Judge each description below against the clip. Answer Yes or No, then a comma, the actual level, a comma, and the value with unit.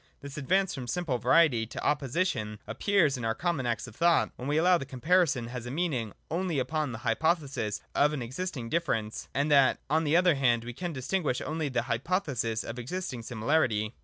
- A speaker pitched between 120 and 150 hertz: Yes, medium, 140 Hz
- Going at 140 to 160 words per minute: No, average, 200 wpm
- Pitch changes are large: Yes, wide, 5.9 semitones